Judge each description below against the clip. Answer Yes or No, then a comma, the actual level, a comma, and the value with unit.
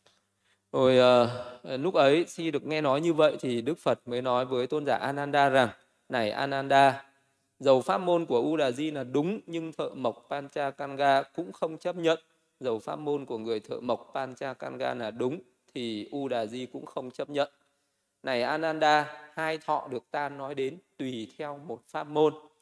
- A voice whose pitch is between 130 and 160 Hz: Yes, medium, 140 Hz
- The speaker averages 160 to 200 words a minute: Yes, average, 180 wpm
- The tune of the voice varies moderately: Yes, average, 3.2 semitones